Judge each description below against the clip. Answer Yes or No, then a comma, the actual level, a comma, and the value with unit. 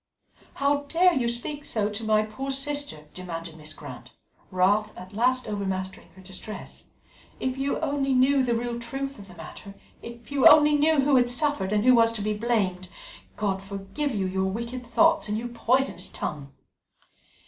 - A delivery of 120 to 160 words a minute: No, average, 175 wpm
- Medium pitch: No, high, 235 Hz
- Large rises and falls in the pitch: Yes, wide, 5.7 semitones